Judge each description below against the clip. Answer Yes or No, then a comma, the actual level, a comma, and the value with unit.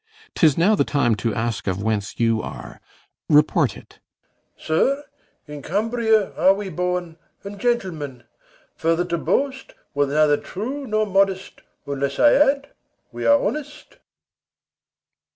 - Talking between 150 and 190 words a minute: No, slow, 135 wpm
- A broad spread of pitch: Yes, wide, 8.0 semitones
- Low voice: No, medium, 180 Hz